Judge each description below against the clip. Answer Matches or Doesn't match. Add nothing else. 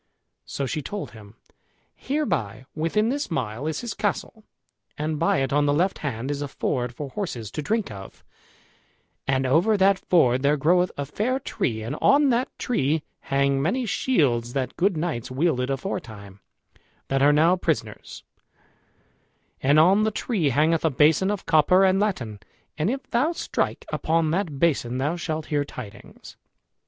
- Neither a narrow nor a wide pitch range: Doesn't match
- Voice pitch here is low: Doesn't match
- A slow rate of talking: Doesn't match